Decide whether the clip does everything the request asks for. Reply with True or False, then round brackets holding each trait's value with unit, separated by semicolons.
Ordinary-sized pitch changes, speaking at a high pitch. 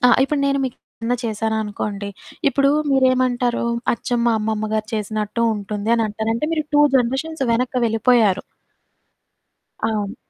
True (3.1 semitones; 230 Hz)